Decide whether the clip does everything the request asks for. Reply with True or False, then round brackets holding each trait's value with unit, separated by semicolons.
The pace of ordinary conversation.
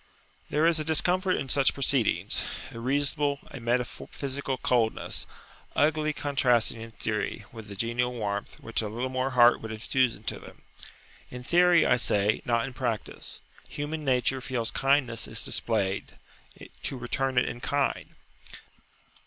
True (145 wpm)